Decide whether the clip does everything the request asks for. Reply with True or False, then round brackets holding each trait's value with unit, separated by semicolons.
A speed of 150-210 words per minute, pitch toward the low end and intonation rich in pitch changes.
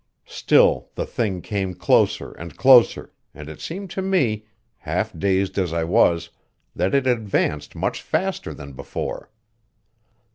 False (140 wpm; 95 Hz; 6.1 semitones)